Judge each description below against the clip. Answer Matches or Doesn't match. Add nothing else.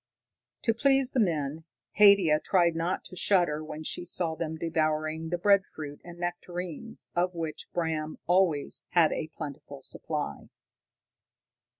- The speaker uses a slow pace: Matches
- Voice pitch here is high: Doesn't match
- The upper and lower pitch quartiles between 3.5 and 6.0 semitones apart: Doesn't match